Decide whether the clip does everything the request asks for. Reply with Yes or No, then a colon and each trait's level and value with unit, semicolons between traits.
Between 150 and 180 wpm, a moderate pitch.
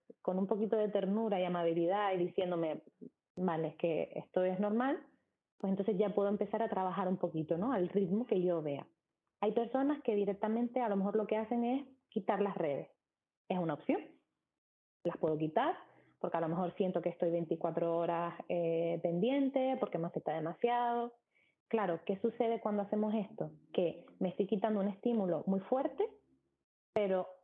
No: average, 175 wpm; high, 200 Hz